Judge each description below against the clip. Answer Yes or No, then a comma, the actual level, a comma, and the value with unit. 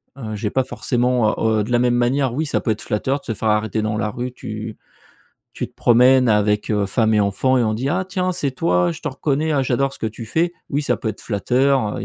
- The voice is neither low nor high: No, low, 120 Hz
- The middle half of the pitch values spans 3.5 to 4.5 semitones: Yes, average, 3.8 semitones